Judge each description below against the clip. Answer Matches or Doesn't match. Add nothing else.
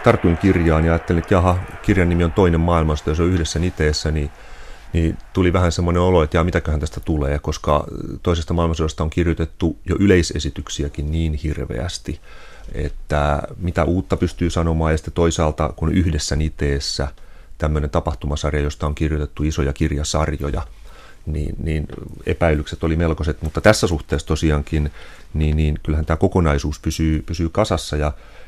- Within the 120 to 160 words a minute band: Matches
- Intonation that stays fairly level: Matches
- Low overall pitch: Matches